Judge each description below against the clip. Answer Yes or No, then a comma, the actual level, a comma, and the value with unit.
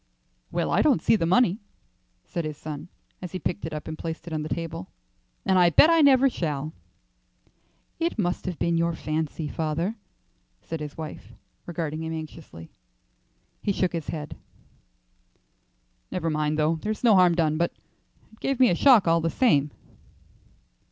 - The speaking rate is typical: Yes, average, 170 wpm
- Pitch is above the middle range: No, medium, 165 Hz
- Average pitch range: Yes, average, 3.0 semitones